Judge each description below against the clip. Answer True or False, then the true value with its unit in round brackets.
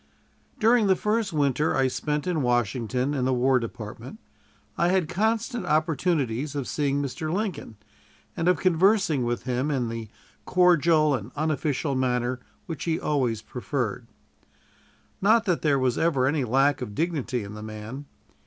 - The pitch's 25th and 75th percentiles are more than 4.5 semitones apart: True (5.2 semitones)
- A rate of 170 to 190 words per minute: False (155 wpm)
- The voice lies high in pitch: False (145 Hz)